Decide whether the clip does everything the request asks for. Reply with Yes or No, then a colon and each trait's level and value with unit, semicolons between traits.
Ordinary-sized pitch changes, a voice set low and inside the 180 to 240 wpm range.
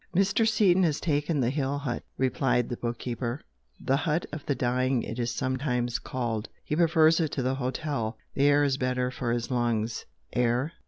Yes: average, 3.5 semitones; low, 130 Hz; average, 190 wpm